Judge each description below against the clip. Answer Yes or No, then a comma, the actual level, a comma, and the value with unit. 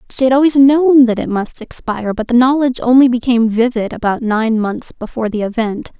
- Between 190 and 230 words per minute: Yes, average, 200 wpm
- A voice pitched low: No, high, 240 Hz